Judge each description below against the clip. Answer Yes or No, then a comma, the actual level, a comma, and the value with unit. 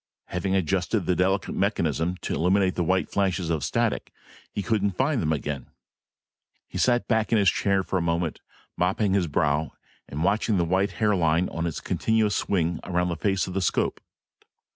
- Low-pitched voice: Yes, very low, 95 Hz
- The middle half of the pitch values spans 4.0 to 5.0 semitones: No, average, 3.1 semitones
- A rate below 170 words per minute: No, average, 180 wpm